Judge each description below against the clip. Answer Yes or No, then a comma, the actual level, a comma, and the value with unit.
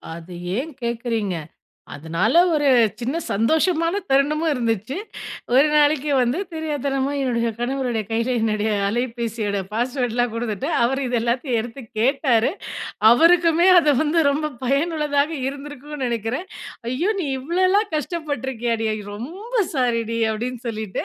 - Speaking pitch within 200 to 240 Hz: No, very high, 255 Hz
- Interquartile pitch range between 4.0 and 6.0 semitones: Yes, average, 4.6 semitones